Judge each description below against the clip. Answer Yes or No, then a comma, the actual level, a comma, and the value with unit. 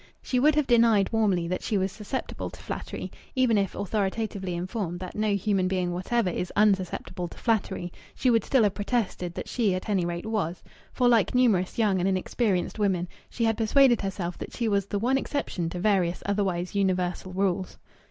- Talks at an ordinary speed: Yes, average, 190 wpm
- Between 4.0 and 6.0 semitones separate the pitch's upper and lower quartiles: No, average, 3.6 semitones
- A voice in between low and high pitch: No, high, 200 Hz